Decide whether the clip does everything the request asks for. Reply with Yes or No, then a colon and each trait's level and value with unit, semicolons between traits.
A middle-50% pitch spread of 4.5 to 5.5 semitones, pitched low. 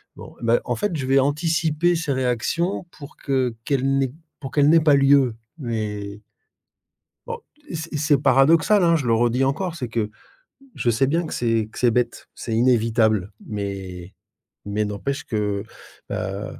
Yes: average, 5.2 semitones; low, 130 Hz